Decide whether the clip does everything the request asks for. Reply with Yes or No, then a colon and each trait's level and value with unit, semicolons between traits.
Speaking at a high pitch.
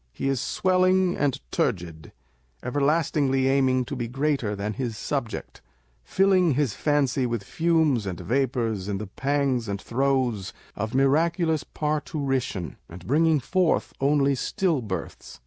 No: low, 135 Hz